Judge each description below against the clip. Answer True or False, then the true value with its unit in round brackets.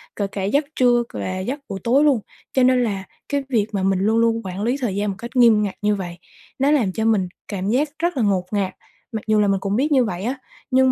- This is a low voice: False (220 Hz)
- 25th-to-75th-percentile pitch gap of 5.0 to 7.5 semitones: False (4.4 semitones)